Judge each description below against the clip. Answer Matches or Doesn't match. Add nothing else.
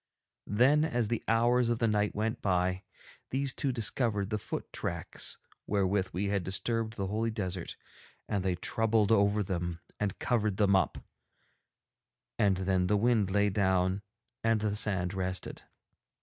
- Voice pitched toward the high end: Doesn't match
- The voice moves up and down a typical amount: Matches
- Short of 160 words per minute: Matches